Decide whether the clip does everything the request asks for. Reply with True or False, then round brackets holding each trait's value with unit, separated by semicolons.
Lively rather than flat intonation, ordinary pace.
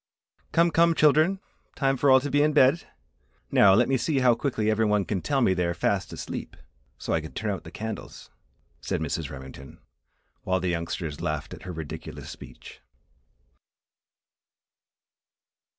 True (8.2 semitones; 165 wpm)